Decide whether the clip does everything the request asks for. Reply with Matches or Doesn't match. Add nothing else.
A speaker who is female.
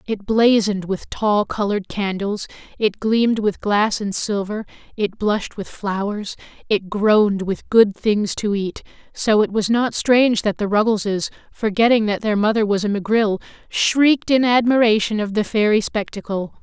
Matches